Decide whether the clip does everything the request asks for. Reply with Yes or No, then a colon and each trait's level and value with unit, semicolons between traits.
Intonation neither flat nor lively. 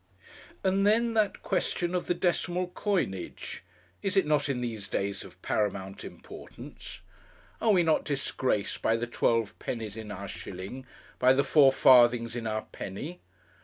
No: wide, 8.4 semitones